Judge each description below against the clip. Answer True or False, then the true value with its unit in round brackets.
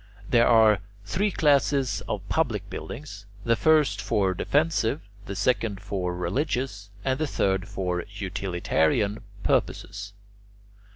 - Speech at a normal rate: False (115 wpm)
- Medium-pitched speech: False (105 Hz)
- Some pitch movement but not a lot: False (5.8 semitones)